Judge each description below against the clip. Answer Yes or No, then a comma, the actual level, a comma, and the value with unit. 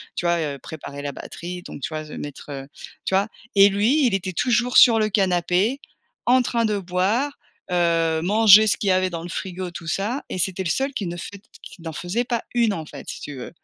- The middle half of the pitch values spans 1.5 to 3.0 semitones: No, average, 4.4 semitones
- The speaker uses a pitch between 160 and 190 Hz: Yes, medium, 185 Hz